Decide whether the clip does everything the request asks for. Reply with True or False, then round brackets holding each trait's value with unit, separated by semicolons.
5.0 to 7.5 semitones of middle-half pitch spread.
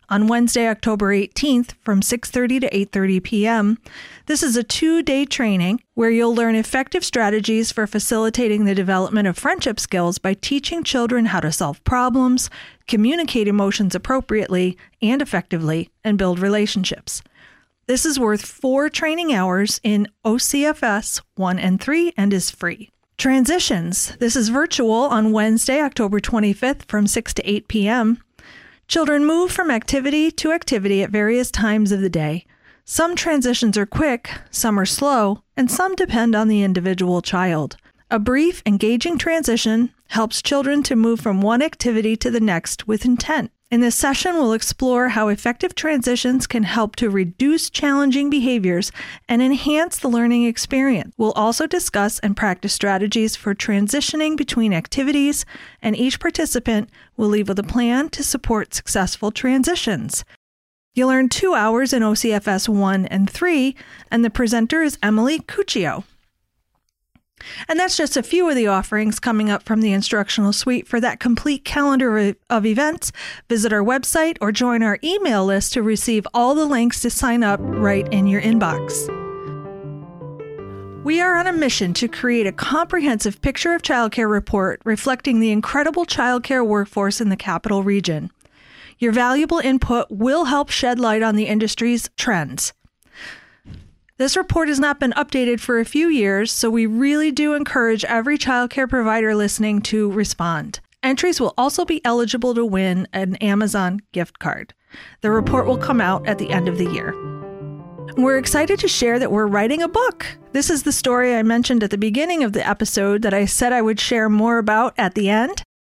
False (4.6 semitones)